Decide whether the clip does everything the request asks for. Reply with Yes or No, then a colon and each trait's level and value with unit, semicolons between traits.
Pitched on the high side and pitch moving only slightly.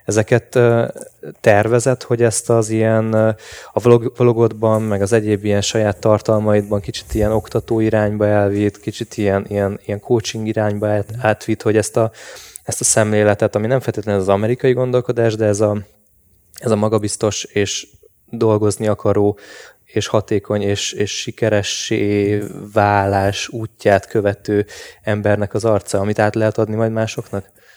No: low, 110 Hz; narrow, 1.7 semitones